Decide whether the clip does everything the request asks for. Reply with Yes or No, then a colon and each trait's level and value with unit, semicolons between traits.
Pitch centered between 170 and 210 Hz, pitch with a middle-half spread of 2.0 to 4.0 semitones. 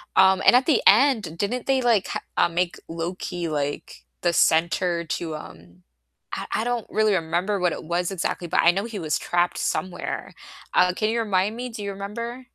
No: medium, 185 Hz; average, 4.4 semitones